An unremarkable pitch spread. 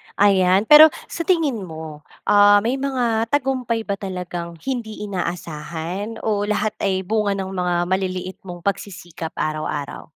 Yes: average, 4.0 semitones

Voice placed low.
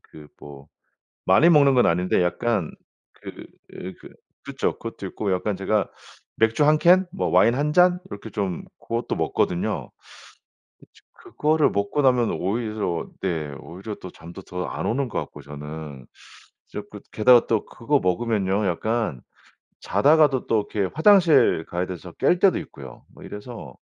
Yes: low, 105 Hz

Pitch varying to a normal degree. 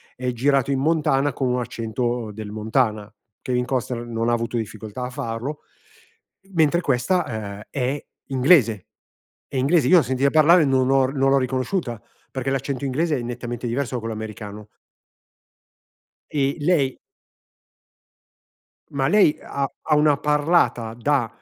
Yes: average, 3.3 semitones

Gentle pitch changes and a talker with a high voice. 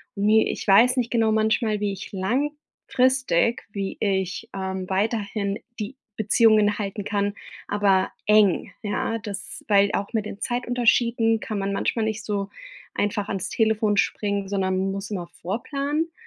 Yes: narrow, 2.3 semitones; high, 210 Hz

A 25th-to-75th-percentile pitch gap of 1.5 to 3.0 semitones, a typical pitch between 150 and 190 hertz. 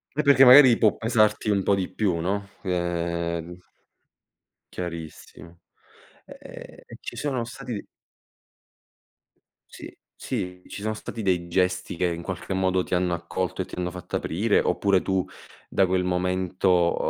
No: average, 2.7 semitones; very low, 95 Hz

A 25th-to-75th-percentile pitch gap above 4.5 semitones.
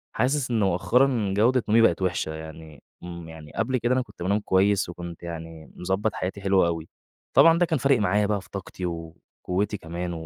Yes: average, 5.0 semitones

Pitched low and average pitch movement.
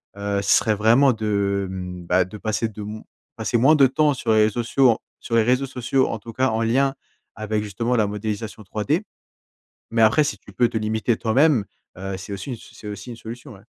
Yes: low, 110 Hz; average, 3.1 semitones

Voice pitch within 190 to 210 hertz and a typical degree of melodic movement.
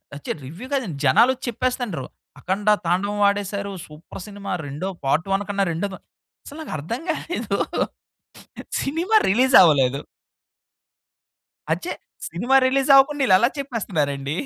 No: high, 200 Hz; wide, 7.6 semitones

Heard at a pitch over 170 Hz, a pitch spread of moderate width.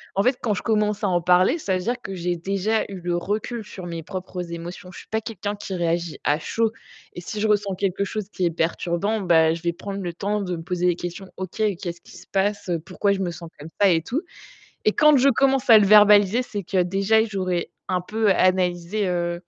Yes: high, 190 Hz; average, 3.1 semitones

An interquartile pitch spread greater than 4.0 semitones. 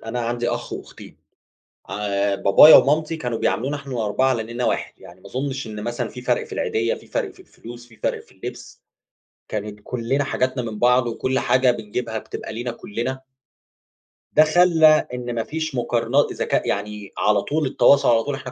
No: average, 3.2 semitones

